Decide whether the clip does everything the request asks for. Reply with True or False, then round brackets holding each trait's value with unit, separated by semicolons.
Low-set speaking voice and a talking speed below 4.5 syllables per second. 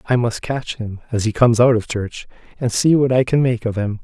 False (120 Hz; 5.5 syllables/s)